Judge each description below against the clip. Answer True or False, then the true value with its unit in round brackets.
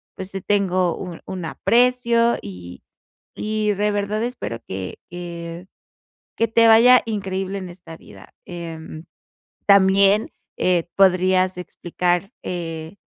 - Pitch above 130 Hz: True (185 Hz)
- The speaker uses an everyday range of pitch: True (3.3 semitones)